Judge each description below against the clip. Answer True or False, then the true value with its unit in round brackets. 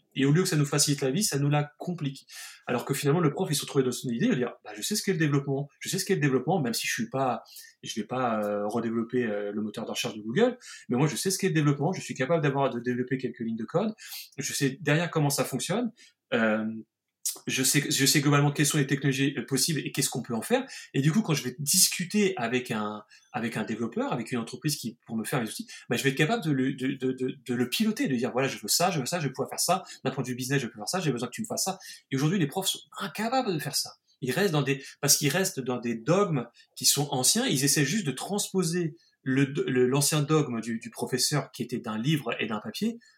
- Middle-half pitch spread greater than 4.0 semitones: True (5.6 semitones)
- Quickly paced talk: True (280 wpm)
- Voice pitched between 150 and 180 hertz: False (140 Hz)